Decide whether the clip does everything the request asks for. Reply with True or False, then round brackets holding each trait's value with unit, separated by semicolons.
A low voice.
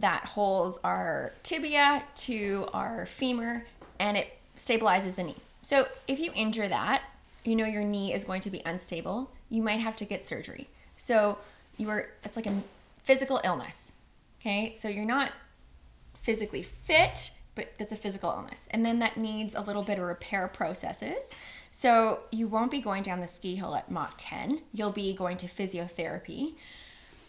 False (215 Hz)